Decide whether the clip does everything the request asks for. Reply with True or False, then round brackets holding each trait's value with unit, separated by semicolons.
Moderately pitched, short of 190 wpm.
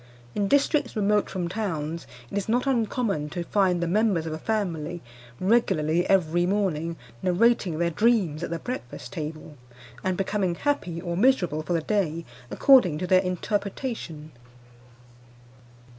True (180 Hz; 145 wpm)